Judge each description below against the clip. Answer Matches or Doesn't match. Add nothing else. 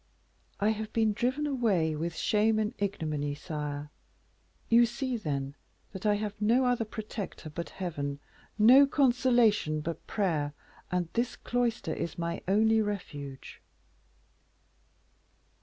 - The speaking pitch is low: Doesn't match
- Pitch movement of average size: Doesn't match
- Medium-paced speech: Doesn't match